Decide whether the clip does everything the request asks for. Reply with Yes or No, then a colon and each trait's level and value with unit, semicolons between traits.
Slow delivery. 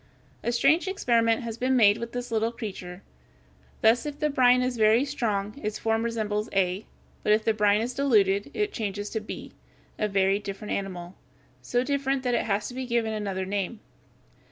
No: average, 180 wpm